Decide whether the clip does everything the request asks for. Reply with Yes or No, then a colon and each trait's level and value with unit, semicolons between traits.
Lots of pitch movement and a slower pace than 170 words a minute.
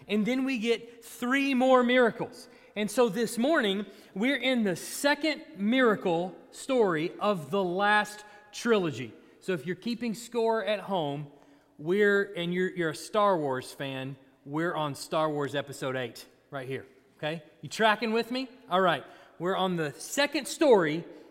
Yes: wide, 7.1 semitones; average, 160 wpm